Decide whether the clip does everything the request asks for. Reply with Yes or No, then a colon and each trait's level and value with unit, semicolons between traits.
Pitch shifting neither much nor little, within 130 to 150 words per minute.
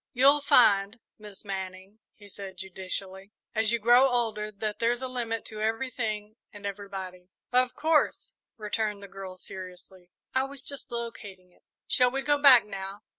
No: average, 4.0 semitones; average, 160 wpm